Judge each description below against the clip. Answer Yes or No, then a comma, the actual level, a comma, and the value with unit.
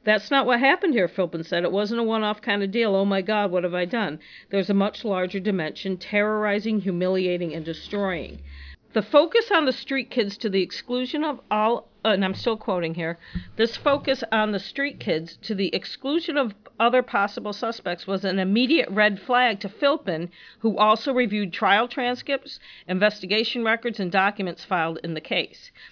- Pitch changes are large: No, average, 4.1 semitones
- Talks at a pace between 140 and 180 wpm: No, average, 190 wpm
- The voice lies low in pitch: No, high, 210 Hz